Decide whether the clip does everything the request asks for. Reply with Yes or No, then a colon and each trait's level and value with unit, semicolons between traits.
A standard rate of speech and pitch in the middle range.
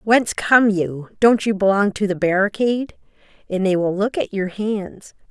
No: average, 180 wpm; high, 205 Hz